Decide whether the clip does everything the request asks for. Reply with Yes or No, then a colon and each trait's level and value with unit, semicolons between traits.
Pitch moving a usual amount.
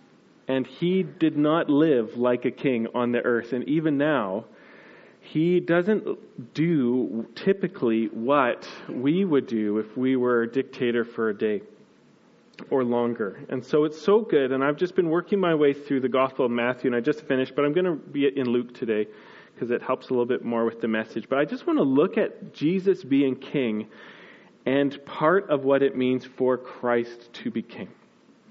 Yes: average, 4.6 semitones